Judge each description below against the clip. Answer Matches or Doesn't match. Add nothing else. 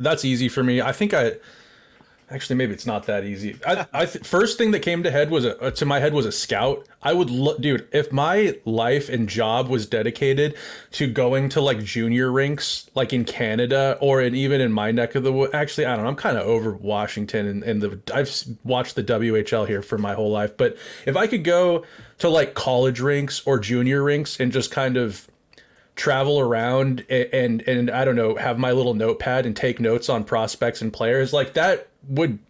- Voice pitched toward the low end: Matches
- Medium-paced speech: Doesn't match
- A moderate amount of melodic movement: Matches